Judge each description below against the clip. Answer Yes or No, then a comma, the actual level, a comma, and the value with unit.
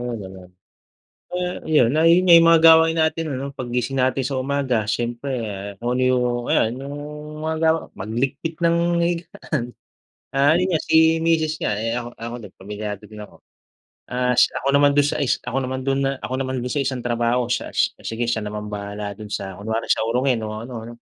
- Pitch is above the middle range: No, low, 130 Hz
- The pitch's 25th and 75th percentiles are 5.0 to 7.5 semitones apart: Yes, average, 5.3 semitones